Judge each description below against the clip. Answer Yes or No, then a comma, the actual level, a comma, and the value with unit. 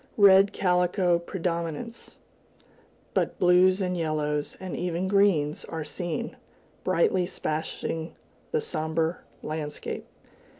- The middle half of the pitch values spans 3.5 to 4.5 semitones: No, average, 2.9 semitones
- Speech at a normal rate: No, slow, 95 wpm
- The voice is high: No, medium, 175 Hz